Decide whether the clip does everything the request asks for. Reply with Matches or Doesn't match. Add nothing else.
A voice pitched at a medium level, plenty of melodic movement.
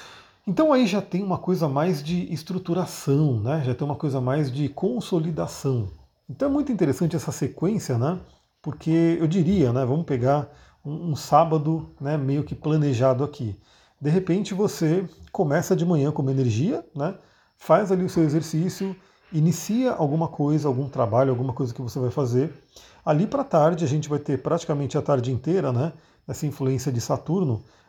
Doesn't match